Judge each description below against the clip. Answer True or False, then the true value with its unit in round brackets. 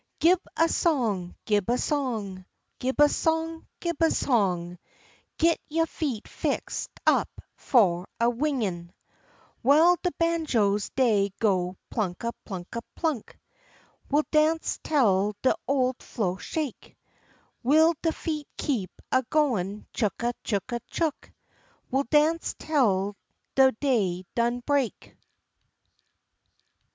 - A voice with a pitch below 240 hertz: False (250 Hz)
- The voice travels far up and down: True (7.1 semitones)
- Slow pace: True (115 wpm)